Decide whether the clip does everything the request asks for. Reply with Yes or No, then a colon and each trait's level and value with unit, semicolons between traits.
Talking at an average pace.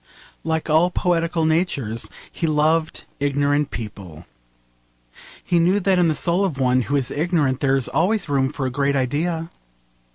Yes: average, 160 wpm